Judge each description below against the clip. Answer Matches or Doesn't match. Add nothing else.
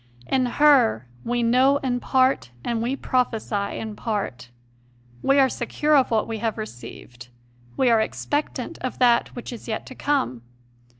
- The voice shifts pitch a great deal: Doesn't match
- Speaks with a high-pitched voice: Matches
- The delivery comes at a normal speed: Matches